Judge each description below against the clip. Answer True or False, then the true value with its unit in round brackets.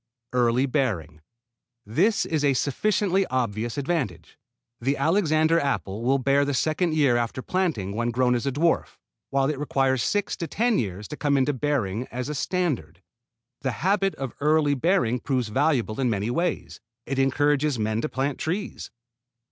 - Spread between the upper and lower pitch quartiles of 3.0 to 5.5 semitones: True (4.7 semitones)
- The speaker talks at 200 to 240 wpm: False (165 wpm)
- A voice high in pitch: False (135 Hz)